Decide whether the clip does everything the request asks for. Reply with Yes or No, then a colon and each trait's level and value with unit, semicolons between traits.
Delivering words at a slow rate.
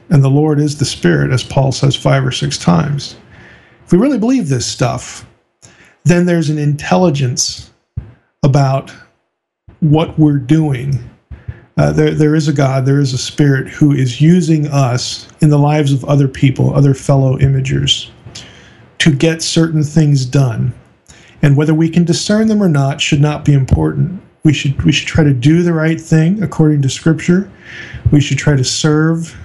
No: average, 175 wpm